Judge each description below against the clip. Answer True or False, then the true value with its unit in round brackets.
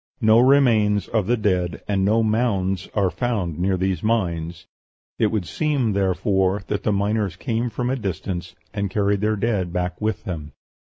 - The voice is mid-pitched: False (100 Hz)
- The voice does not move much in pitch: False (3.2 semitones)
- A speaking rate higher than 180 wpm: False (170 wpm)